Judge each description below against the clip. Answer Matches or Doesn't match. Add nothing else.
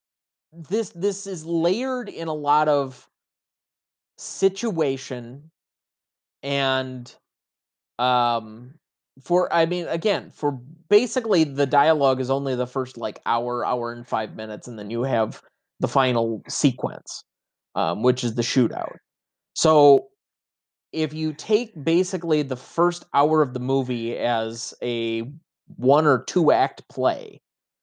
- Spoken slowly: Matches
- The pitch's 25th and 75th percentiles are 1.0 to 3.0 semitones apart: Doesn't match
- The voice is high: Doesn't match